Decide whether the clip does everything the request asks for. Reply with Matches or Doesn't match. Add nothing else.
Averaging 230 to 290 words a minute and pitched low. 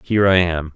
Matches